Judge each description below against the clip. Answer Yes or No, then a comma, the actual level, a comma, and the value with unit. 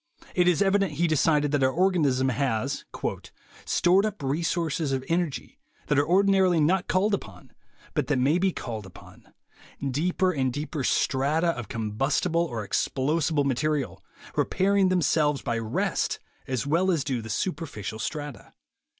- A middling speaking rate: Yes, average, 150 wpm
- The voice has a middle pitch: Yes, medium, 150 Hz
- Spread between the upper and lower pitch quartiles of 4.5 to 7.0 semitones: Yes, average, 5.1 semitones